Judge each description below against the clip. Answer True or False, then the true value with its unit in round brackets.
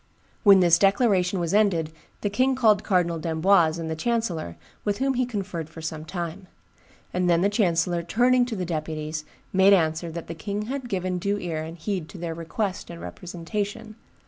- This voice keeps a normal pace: True (185 wpm)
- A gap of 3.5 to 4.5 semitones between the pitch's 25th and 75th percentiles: True (3.8 semitones)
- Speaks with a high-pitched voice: False (180 Hz)